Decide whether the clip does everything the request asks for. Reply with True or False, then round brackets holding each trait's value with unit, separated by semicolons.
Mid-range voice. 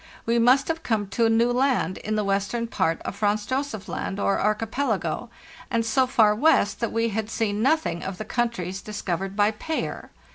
False (220 Hz)